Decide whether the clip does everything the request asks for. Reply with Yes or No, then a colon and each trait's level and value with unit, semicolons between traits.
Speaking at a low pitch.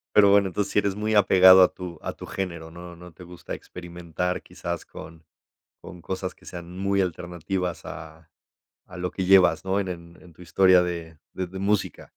Yes: very low, 90 Hz